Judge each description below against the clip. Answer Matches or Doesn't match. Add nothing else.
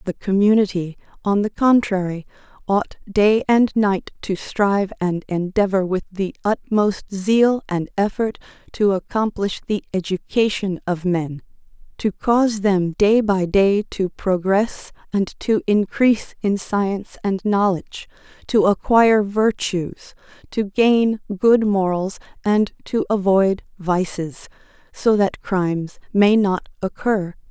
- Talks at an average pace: Doesn't match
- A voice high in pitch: Matches